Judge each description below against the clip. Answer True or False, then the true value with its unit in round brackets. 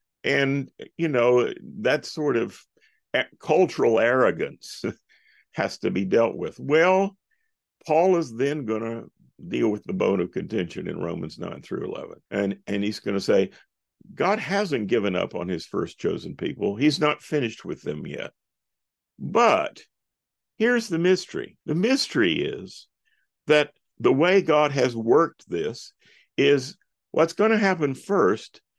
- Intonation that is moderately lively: False (7.3 semitones)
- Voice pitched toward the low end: False (160 Hz)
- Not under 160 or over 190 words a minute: False (150 wpm)